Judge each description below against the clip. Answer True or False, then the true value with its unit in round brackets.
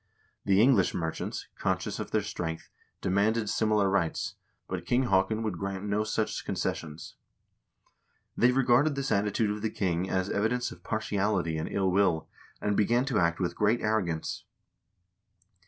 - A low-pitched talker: True (100 Hz)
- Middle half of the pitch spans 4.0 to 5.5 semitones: False (3.0 semitones)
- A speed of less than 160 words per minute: True (150 wpm)